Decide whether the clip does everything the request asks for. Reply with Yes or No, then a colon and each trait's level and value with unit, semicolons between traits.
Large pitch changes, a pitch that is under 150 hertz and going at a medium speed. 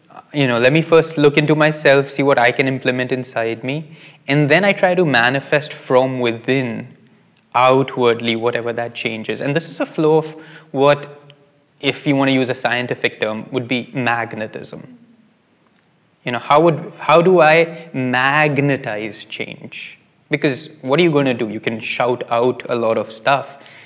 No: average, 4.0 semitones; medium, 140 Hz; average, 175 wpm